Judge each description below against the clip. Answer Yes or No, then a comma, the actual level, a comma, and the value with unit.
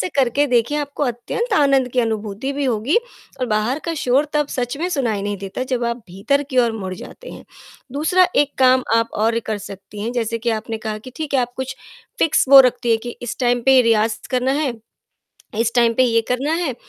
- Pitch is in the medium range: No, high, 245 Hz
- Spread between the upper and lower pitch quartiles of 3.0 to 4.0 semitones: Yes, average, 3.4 semitones